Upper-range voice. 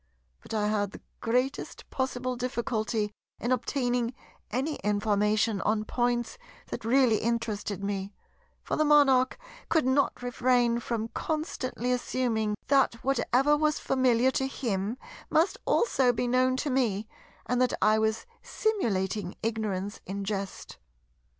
Yes: high, 240 Hz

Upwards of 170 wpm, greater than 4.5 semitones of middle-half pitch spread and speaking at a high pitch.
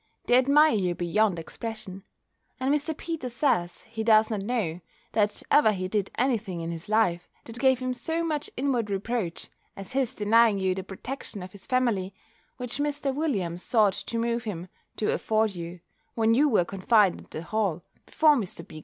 Yes: average, 185 wpm; average, 5.2 semitones; high, 220 Hz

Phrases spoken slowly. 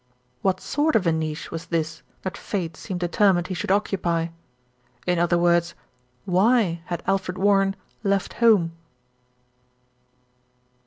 Yes: slow, 130 wpm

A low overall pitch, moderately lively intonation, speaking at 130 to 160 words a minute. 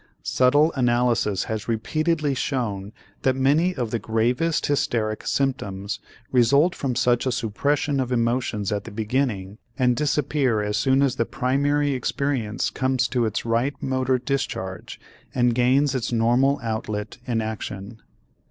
Yes: low, 125 Hz; average, 3.7 semitones; average, 140 wpm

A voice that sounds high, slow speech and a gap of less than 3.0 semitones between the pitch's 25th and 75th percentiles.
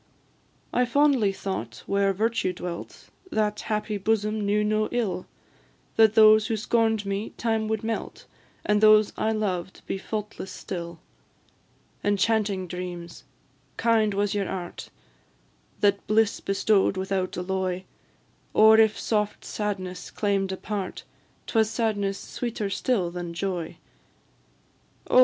Yes: high, 205 Hz; slow, 125 wpm; narrow, 2.5 semitones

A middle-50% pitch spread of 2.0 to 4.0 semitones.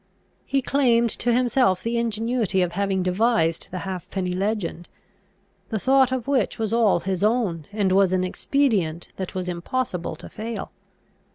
No: average, 4.4 semitones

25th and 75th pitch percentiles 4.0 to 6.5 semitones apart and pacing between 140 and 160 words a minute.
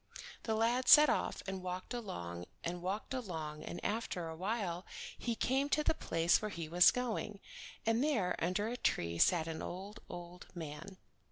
No: average, 5.1 semitones; average, 170 wpm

